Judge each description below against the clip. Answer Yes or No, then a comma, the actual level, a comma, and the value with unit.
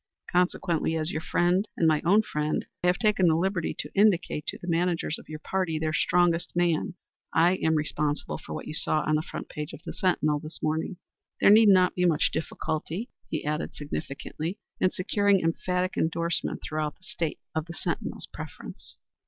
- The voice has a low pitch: No, medium, 170 Hz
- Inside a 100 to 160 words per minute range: No, average, 185 wpm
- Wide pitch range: No, average, 2.8 semitones